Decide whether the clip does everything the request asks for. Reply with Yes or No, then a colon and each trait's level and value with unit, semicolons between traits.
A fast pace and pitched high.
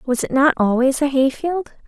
Yes: fast, 225 wpm; very high, 275 Hz